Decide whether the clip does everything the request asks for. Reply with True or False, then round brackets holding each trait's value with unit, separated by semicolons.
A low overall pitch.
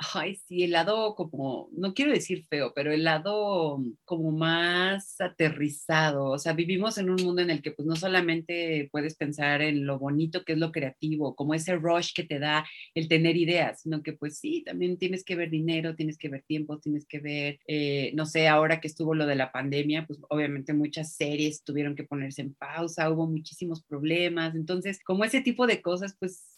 False (160 Hz)